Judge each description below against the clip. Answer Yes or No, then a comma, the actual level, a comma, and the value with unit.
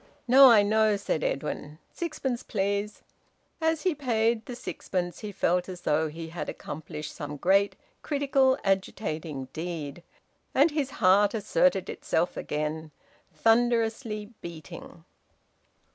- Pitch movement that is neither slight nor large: No, wide, 6.8 semitones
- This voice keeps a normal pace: No, slow, 120 wpm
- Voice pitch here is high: Yes, high, 205 Hz